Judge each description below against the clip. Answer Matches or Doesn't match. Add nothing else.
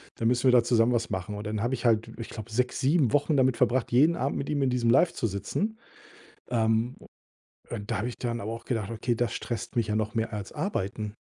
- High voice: Doesn't match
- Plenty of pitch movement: Doesn't match